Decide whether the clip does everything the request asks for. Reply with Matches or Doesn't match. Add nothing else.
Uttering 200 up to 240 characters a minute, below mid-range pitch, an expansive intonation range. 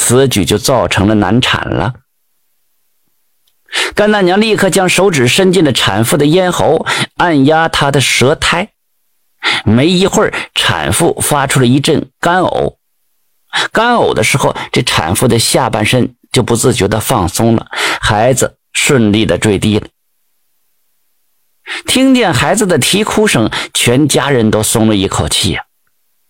Matches